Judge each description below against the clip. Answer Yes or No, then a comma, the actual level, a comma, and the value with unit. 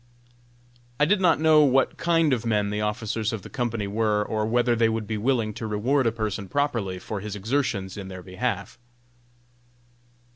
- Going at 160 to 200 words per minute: Yes, average, 180 wpm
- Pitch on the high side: No, low, 110 Hz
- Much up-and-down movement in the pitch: No, average, 3.6 semitones